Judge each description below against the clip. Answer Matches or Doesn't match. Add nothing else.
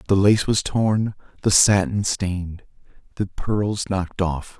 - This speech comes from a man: Matches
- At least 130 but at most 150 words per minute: Matches